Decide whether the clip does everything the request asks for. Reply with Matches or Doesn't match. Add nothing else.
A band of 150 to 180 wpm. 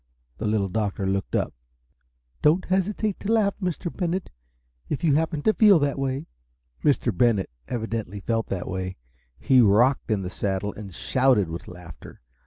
Matches